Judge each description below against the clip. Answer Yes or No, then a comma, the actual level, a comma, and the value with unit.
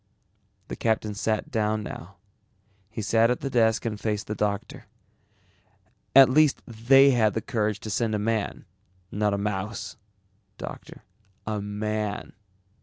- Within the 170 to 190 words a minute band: No, average, 140 wpm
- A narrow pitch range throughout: Yes, narrow, 1.7 semitones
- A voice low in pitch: Yes, low, 110 Hz